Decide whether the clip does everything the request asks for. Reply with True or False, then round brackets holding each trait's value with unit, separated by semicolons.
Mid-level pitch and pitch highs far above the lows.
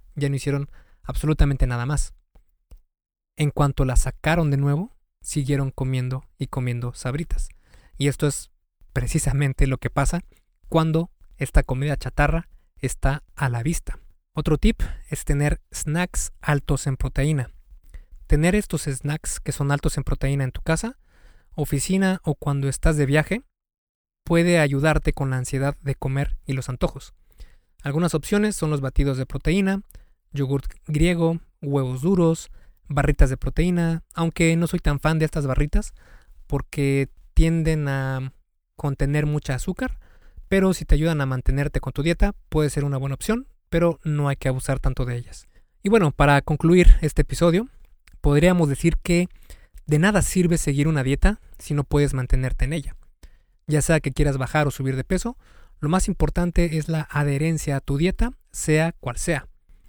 False (145 Hz; 3.5 semitones)